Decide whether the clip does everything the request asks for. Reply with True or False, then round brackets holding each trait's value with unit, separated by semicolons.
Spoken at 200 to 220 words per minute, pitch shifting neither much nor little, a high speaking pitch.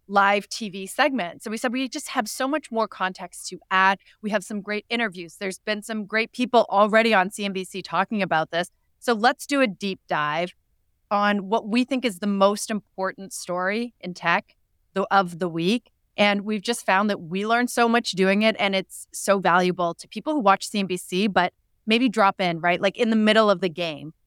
True (205 wpm; 3.3 semitones; 200 Hz)